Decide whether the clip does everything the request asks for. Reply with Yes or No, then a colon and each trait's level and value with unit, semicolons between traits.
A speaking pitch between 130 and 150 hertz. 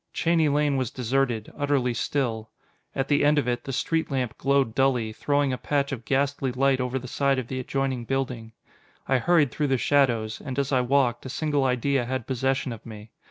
Yes: low, 135 Hz